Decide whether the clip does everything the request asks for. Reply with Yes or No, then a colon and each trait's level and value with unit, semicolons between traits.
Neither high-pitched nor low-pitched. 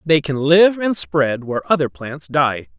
Yes: medium, 145 Hz